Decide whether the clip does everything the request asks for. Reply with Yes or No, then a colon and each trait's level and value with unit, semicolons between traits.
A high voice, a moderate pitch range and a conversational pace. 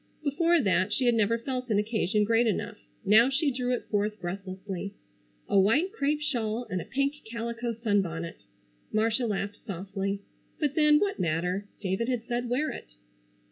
Yes: high, 225 Hz; average, 4.3 semitones; average, 165 wpm